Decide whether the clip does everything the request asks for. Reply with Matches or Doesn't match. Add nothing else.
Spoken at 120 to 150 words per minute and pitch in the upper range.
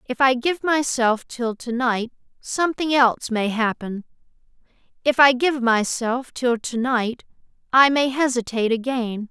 Matches